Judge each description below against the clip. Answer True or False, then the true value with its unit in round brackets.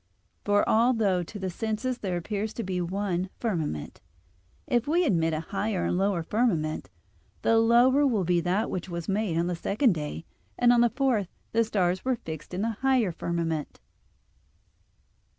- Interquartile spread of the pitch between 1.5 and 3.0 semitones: False (4.9 semitones)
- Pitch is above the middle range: True (200 Hz)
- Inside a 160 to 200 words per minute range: True (170 wpm)